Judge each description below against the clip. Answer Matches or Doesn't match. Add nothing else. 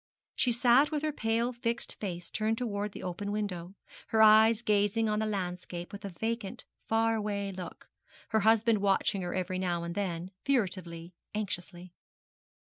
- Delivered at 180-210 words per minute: Doesn't match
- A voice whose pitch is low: Doesn't match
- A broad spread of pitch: Doesn't match